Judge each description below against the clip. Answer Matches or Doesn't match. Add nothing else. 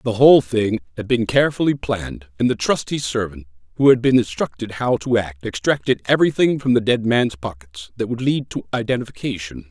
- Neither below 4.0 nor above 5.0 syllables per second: Doesn't match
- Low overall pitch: Matches